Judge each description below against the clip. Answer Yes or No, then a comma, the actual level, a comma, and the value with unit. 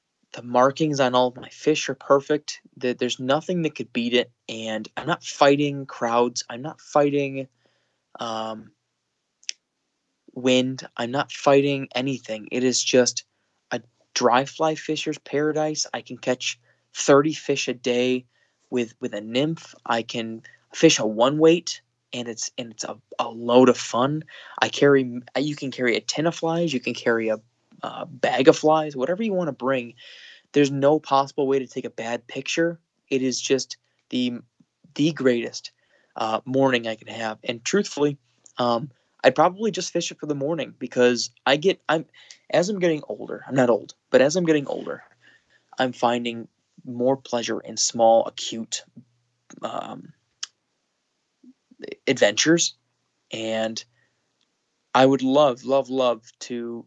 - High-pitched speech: No, low, 130 Hz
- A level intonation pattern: No, average, 3.6 semitones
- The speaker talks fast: No, average, 155 wpm